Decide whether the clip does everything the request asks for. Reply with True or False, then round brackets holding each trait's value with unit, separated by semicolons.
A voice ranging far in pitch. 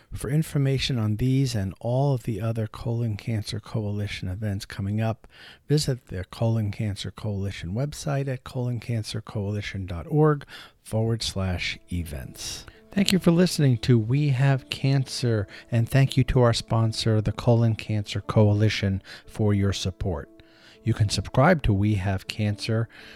False (3.7 semitones)